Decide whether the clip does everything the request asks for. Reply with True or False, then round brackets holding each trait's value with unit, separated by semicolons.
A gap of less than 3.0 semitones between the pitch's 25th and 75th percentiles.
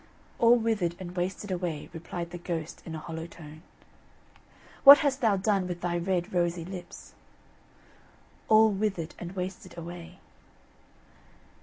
True (2.5 semitones)